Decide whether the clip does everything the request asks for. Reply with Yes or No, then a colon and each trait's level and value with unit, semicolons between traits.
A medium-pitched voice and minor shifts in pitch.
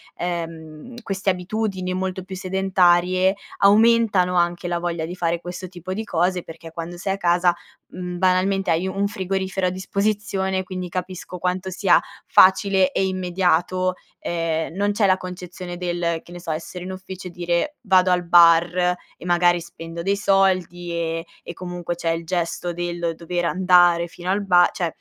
Yes: medium, 180 Hz; narrow, 1.6 semitones